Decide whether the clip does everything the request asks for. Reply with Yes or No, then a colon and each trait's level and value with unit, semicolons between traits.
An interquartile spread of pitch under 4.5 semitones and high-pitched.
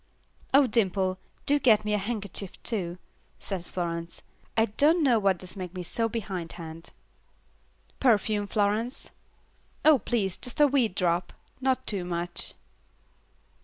No: average, 4.8 semitones; high, 205 Hz